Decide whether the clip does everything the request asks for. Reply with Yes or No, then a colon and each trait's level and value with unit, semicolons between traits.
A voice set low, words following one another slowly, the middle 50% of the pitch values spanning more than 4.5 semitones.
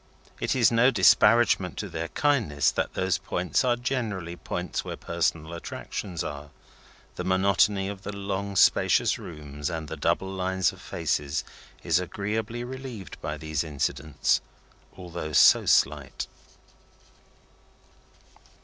Yes: very low, 95 Hz; slow, 125 wpm; average, 5.0 semitones